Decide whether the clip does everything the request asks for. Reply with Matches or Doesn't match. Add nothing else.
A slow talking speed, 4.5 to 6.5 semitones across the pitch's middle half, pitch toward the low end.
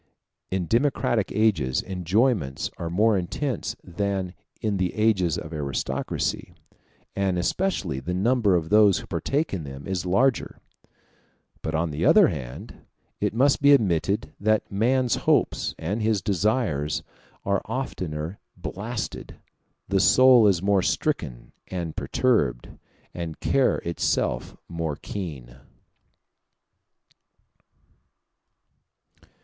Matches